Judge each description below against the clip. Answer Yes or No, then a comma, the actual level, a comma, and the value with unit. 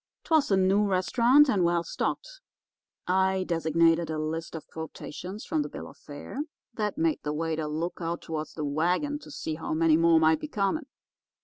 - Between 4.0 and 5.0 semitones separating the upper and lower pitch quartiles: Yes, average, 4.7 semitones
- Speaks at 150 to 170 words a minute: No, average, 185 wpm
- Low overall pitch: No, medium, 170 Hz